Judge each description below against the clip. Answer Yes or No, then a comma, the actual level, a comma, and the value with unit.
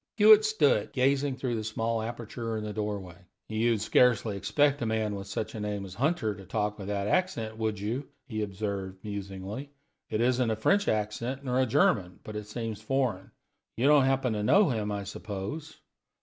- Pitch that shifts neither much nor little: Yes, average, 3.8 semitones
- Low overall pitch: Yes, low, 110 Hz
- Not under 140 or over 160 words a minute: No, average, 190 wpm